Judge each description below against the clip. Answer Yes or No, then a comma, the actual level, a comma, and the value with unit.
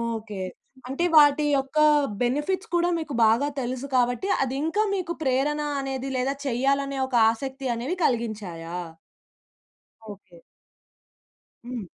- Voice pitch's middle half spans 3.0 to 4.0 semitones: Yes, average, 3.6 semitones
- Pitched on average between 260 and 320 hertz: Yes, very high, 265 Hz